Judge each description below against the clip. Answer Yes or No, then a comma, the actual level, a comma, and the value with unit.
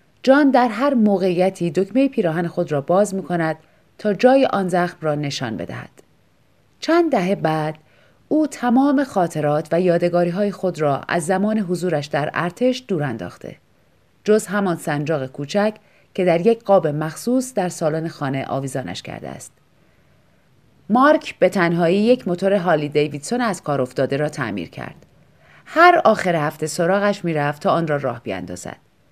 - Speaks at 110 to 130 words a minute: No, fast, 155 wpm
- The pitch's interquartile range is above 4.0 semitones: Yes, wide, 5.6 semitones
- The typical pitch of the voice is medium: Yes, medium, 180 Hz